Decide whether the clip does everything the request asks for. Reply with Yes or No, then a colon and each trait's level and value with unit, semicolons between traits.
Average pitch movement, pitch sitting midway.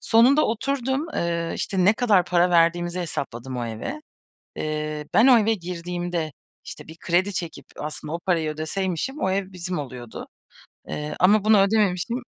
Yes: average, 4.8 semitones; medium, 175 Hz